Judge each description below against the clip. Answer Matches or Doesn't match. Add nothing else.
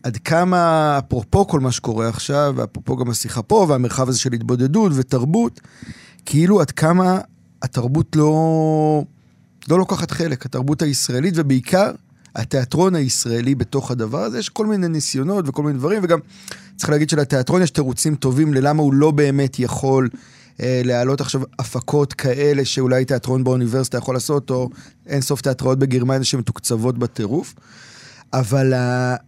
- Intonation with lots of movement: Doesn't match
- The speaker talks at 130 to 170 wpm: Matches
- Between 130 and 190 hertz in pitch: Matches